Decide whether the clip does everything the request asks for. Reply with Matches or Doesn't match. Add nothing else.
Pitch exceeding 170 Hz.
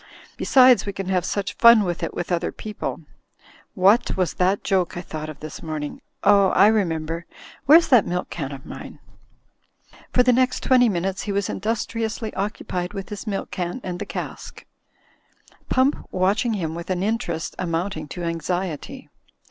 Matches